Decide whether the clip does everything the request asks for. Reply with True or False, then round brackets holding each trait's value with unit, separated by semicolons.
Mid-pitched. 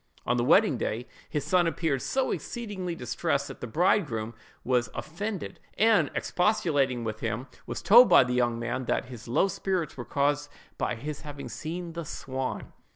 True (145 Hz)